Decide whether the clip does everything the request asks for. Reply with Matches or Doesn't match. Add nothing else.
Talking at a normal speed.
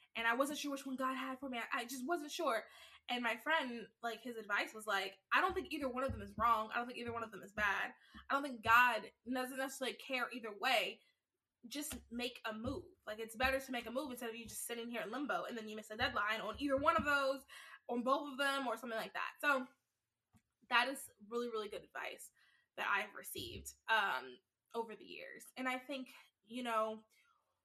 Doesn't match